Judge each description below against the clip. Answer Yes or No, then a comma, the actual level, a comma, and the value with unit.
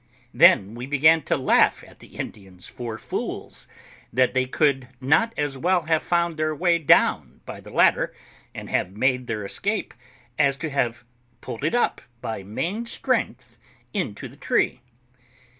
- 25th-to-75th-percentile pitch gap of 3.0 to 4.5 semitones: No, wide, 5.4 semitones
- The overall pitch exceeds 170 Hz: No, low, 135 Hz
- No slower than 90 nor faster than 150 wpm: No, average, 160 wpm